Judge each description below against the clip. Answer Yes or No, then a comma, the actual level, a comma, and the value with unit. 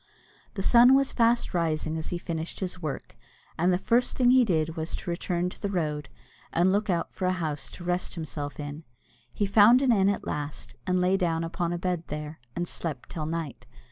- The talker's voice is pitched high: No, medium, 175 Hz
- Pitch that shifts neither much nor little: Yes, average, 3.5 semitones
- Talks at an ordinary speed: No, fast, 210 wpm